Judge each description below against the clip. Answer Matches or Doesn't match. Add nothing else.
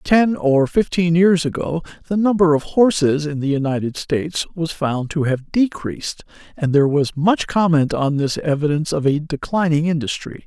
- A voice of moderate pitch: Matches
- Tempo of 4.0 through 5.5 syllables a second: Matches